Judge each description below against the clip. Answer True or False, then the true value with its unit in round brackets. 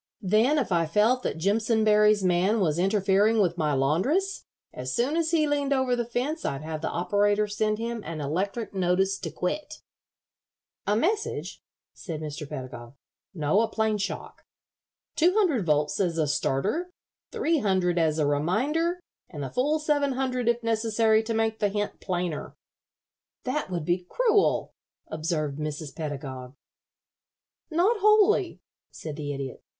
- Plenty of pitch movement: True (7.8 semitones)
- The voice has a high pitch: True (205 Hz)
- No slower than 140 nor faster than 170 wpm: True (150 wpm)